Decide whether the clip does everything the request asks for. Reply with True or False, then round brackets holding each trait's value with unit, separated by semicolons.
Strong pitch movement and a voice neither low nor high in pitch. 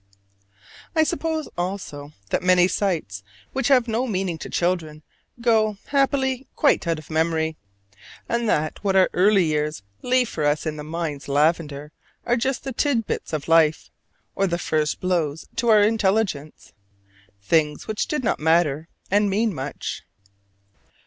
True (6.5 semitones; 180 Hz)